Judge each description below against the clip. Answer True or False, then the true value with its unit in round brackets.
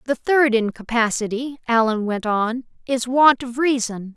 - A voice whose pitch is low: False (240 Hz)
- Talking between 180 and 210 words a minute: False (145 wpm)